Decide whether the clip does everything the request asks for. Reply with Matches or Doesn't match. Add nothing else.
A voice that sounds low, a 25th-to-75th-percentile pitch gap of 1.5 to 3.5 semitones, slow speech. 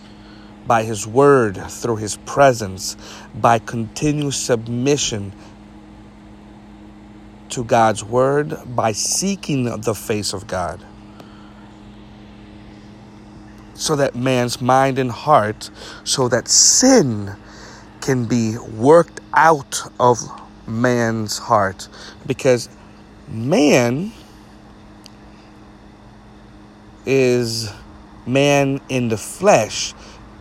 Matches